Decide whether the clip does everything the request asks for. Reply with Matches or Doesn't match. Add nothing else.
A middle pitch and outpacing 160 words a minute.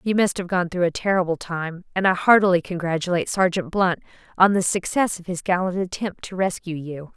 Matches